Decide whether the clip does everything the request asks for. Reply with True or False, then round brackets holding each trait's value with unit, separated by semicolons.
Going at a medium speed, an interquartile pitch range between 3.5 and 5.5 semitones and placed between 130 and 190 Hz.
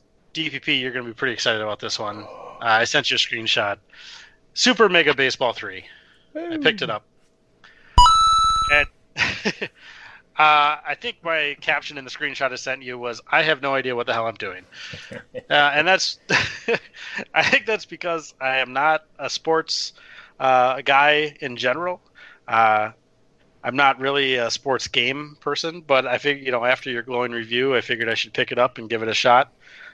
True (180 wpm; 4.1 semitones; 140 Hz)